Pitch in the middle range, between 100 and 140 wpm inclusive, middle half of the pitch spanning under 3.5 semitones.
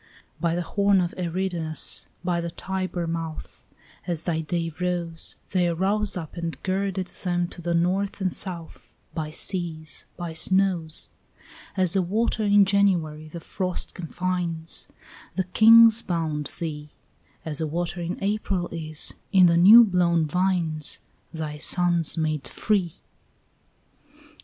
Yes: medium, 175 Hz; slow, 135 wpm; narrow, 2.6 semitones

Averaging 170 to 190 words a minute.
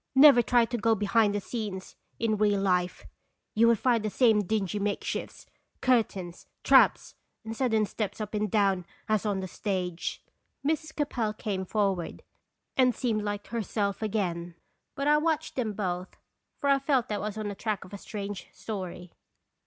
Yes: average, 175 wpm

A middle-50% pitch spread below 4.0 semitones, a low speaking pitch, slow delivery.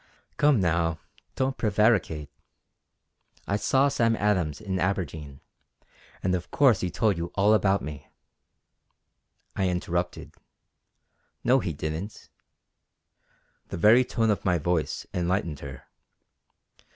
No: average, 4.4 semitones; very low, 95 Hz; slow, 115 wpm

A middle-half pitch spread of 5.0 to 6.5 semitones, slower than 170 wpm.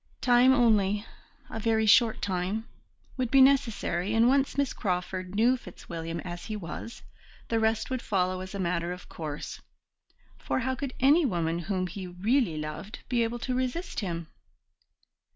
Yes: wide, 5.5 semitones; average, 160 wpm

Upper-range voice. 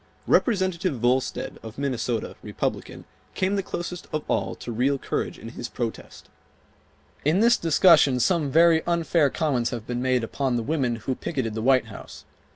No: low, 135 Hz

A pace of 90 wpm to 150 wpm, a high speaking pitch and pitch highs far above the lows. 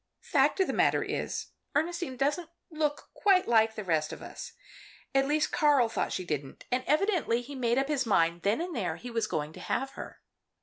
No: fast, 205 wpm; very high, 260 Hz; wide, 5.9 semitones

